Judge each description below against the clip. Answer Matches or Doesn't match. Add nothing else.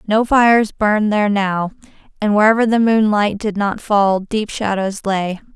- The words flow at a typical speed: Matches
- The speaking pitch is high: Matches